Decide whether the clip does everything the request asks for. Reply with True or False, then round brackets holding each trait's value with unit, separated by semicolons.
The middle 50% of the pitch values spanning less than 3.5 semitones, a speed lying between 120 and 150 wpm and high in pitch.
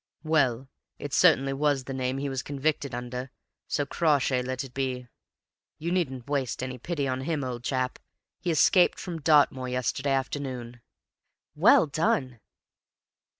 False (2.4 semitones; 145 wpm; 135 Hz)